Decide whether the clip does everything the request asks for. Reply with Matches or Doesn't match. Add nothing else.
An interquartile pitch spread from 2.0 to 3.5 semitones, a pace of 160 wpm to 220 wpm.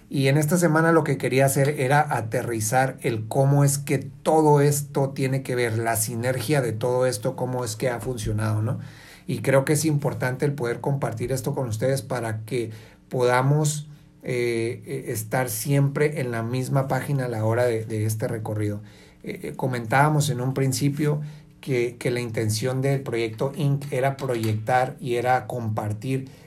Matches